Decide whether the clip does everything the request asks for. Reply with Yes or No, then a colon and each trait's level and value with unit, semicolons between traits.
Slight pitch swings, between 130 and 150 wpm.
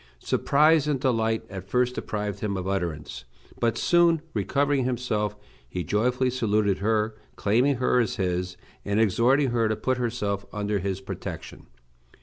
No: average, 3.9 semitones; average, 145 wpm